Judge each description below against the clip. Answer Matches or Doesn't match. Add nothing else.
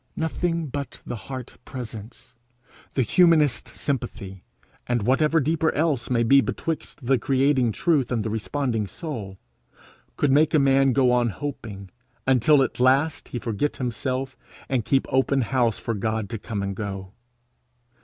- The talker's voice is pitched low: Matches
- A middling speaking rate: Matches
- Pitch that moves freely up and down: Doesn't match